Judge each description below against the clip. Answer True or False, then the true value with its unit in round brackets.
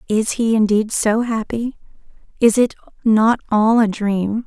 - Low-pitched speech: False (220 Hz)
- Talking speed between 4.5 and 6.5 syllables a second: False (4.0 syllables/s)